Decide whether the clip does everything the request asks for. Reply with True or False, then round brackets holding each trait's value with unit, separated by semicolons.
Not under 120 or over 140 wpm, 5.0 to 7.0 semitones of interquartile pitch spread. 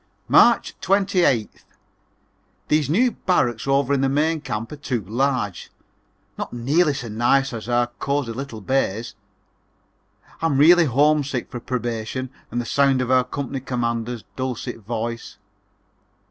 False (135 wpm; 3.2 semitones)